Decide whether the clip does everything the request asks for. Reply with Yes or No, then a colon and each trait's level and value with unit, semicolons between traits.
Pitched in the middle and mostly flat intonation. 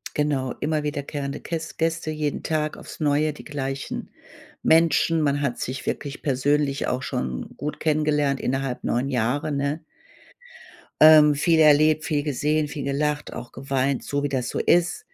Yes: medium, 145 Hz; narrow, 2.0 semitones